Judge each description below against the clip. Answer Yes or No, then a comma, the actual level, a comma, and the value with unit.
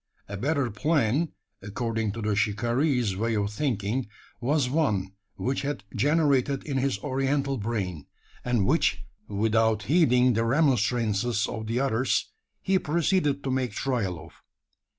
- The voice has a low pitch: Yes, low, 120 Hz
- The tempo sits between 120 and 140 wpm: Yes, slow, 135 wpm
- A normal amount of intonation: Yes, average, 4.6 semitones